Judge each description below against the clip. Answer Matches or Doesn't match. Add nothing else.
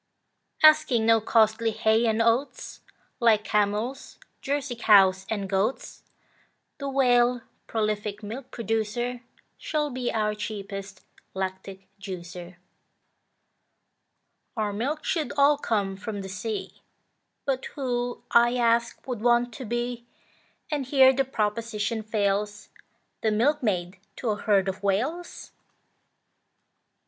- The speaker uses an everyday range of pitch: Matches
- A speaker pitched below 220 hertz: Doesn't match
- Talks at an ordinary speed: Doesn't match